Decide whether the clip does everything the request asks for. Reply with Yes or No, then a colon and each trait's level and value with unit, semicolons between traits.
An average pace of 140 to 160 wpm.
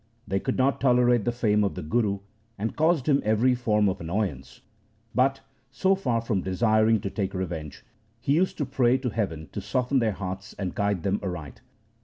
No: average, 190 wpm